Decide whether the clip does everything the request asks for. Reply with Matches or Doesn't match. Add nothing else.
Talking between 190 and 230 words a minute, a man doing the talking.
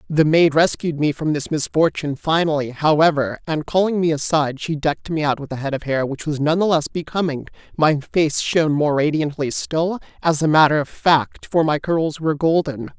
Matches